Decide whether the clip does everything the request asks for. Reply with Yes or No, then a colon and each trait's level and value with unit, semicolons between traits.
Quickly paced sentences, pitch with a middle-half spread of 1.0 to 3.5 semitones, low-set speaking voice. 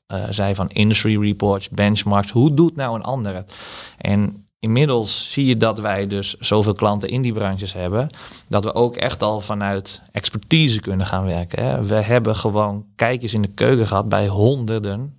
No: average, 180 wpm; average, 3.0 semitones; low, 105 Hz